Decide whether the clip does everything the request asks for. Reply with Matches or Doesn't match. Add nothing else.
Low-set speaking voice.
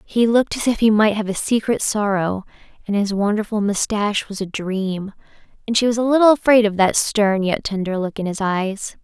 Doesn't match